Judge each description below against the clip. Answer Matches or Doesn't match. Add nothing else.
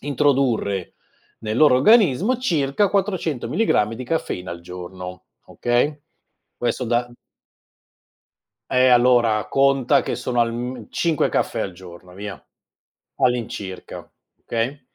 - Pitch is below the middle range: Matches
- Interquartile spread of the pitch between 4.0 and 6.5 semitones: Matches